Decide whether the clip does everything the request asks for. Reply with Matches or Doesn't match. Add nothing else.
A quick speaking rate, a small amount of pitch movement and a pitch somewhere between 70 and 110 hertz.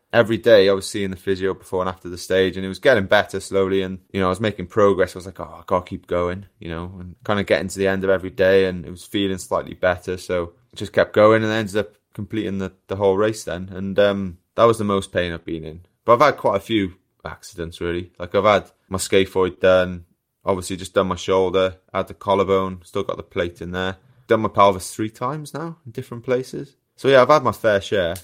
Matches